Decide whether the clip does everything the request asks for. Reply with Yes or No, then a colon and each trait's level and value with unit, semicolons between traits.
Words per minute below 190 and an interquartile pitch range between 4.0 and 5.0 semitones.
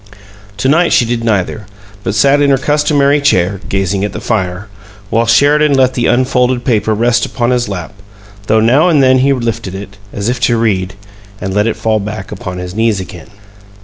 No: average, 195 wpm; average, 4.5 semitones